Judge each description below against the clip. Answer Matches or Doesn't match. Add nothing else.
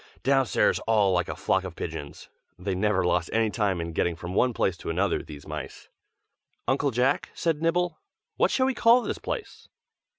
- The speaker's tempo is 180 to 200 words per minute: Matches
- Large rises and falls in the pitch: Matches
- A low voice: Matches